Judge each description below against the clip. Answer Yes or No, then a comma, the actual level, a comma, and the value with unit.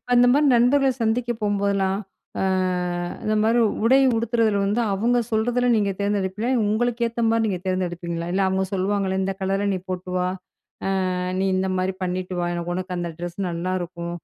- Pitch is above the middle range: Yes, high, 195 Hz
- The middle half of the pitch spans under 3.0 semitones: No, average, 3.7 semitones